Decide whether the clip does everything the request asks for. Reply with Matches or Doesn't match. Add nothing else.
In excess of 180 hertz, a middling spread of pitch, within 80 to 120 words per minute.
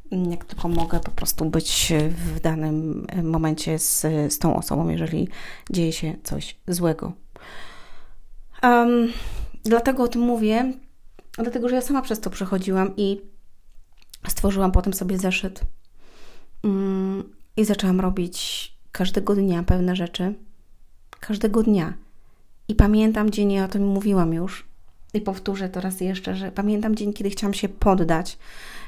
Doesn't match